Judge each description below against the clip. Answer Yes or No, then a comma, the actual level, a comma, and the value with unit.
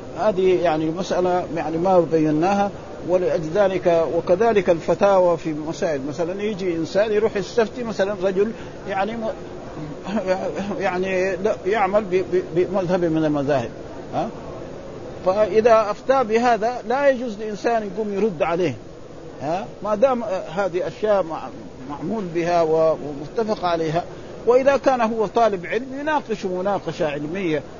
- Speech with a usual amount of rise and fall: Yes, average, 4.1 semitones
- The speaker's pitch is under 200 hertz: Yes, high, 190 Hz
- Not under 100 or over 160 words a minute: Yes, average, 110 wpm